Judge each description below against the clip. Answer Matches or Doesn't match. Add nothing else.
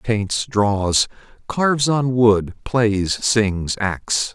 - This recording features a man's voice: Matches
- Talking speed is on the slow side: Matches